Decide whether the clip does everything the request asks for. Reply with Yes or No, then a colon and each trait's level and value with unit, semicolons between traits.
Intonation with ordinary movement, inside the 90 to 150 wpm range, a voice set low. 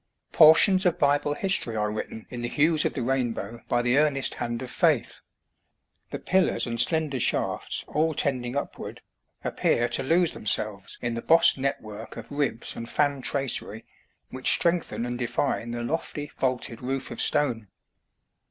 No: average, 4.0 semitones; average, 160 wpm; low, 130 Hz